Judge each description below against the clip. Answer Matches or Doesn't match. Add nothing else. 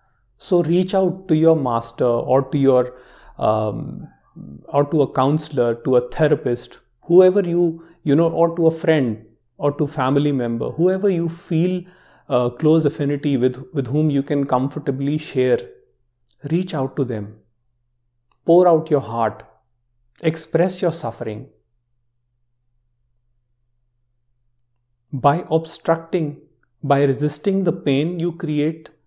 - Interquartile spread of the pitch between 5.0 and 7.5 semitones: Matches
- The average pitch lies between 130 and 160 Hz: Matches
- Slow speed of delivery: Matches